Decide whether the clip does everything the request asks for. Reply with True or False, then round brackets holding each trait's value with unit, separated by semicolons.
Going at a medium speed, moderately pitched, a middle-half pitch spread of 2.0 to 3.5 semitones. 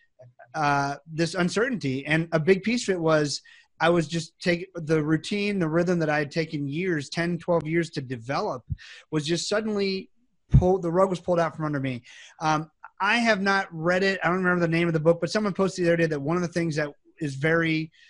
False (225 wpm; 170 Hz; 2.9 semitones)